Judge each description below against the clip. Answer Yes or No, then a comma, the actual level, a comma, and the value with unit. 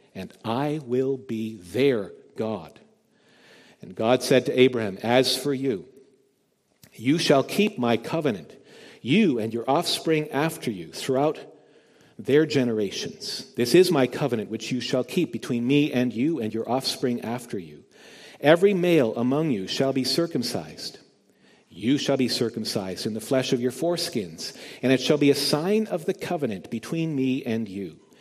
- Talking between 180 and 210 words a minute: No, average, 160 wpm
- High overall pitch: No, low, 130 Hz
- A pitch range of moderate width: Yes, average, 4.1 semitones